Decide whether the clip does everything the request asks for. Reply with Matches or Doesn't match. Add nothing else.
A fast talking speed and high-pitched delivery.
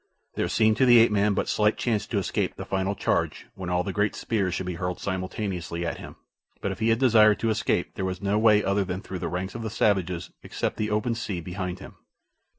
Doesn't match